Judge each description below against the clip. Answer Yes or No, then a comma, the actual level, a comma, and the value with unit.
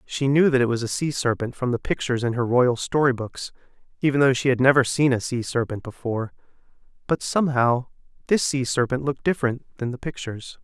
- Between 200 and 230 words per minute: Yes, fast, 205 wpm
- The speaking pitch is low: Yes, low, 130 Hz